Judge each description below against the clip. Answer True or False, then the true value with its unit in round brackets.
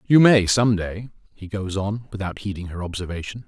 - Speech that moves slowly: False (190 wpm)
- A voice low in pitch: True (100 Hz)